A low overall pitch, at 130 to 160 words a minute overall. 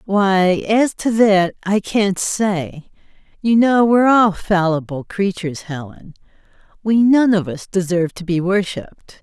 No: high, 195 Hz; average, 145 wpm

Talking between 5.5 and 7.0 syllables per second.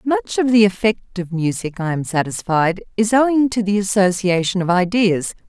No: 4.9 syllables/s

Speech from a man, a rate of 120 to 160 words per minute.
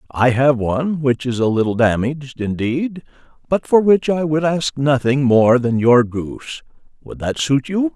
No: male; average, 180 wpm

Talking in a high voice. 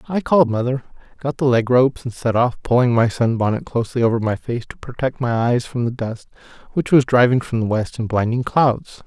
No: low, 125 Hz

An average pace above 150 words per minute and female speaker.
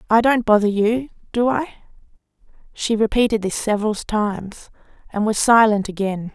No: average, 140 wpm; female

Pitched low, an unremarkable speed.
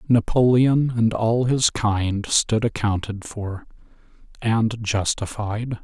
No: low, 110 Hz; slow, 95 wpm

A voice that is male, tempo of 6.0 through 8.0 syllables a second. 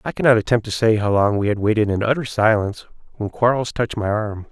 Yes: male; 6.4 syllables/s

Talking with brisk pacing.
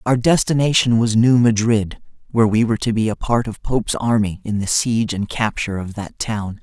Yes: fast, 210 wpm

